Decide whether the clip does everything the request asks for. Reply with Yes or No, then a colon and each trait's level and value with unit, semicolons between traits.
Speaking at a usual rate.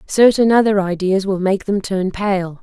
Yes: average, 185 wpm